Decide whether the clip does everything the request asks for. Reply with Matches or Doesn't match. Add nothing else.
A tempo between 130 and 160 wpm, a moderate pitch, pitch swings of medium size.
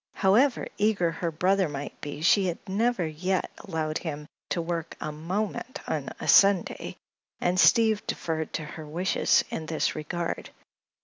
Matches